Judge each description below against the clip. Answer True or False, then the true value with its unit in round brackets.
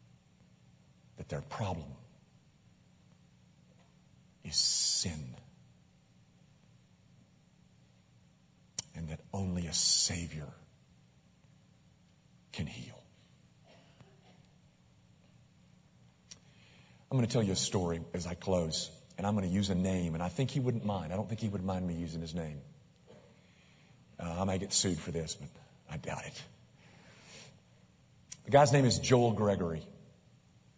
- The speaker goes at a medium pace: False (120 wpm)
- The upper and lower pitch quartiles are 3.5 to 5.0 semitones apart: True (4.4 semitones)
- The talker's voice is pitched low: True (90 Hz)